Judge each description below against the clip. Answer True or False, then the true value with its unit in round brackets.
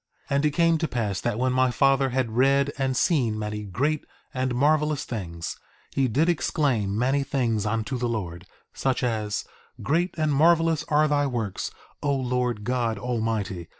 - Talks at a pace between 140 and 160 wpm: False (170 wpm)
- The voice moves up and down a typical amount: True (4.4 semitones)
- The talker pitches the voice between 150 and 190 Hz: False (130 Hz)